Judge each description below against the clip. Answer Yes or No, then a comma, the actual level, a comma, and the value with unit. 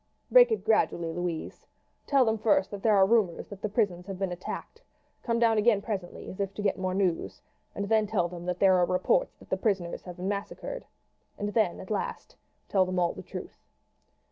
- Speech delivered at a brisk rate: Yes, fast, 210 wpm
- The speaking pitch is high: Yes, high, 200 Hz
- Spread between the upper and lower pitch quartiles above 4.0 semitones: No, average, 3.3 semitones